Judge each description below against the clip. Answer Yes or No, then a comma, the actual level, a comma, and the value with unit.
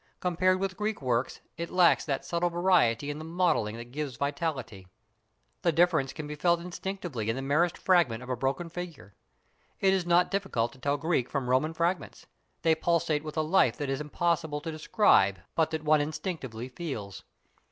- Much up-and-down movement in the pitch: No, average, 4.6 semitones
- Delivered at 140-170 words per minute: No, average, 185 wpm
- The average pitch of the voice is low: No, medium, 155 Hz